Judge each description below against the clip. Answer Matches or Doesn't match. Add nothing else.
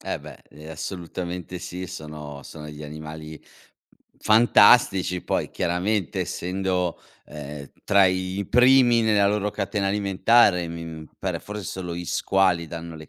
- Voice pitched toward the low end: Matches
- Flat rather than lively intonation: Doesn't match